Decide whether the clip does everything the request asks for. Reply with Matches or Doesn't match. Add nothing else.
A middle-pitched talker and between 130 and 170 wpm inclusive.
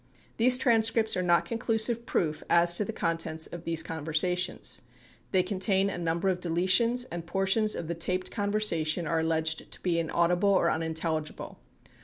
Matches